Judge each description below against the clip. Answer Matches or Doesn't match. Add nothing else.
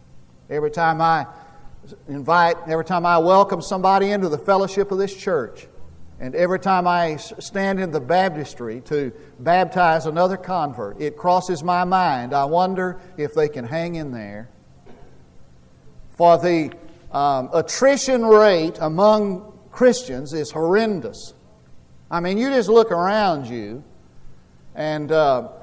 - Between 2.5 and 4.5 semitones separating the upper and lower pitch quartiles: Doesn't match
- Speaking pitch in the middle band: Matches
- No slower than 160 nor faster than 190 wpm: Doesn't match